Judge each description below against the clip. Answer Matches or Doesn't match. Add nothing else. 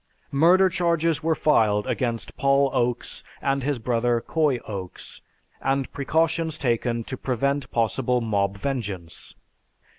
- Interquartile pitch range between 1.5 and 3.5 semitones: Doesn't match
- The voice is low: Matches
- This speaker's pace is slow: Matches